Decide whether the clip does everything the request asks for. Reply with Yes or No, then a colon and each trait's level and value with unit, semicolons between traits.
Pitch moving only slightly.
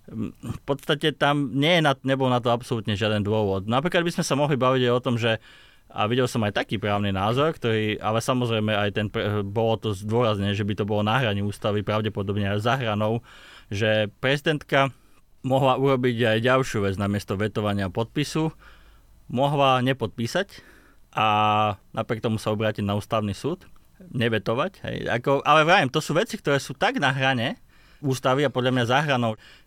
No: average, 4.1 semitones